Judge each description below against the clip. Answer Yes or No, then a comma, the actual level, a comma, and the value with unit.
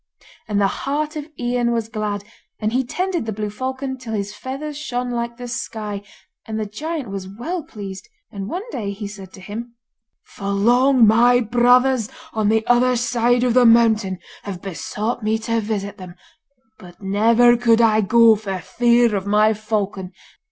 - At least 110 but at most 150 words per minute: No, average, 175 wpm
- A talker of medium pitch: No, high, 225 Hz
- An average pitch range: Yes, average, 3.1 semitones